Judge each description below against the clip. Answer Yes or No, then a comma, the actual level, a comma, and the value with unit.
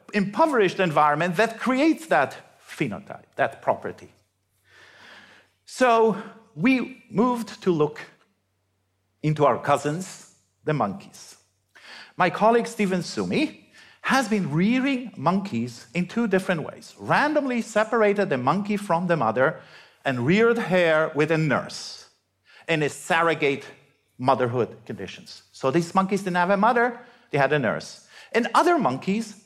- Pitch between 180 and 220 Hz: Yes, high, 190 Hz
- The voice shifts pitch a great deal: Yes, wide, 7.0 semitones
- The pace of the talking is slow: Yes, slow, 125 wpm